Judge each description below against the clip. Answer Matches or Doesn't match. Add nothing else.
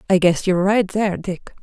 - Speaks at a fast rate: Matches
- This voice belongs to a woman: Matches